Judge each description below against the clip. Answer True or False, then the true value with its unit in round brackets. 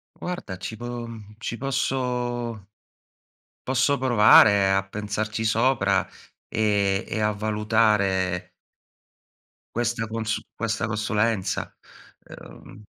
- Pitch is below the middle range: True (110 Hz)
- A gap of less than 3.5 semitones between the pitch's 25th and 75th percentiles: True (2.6 semitones)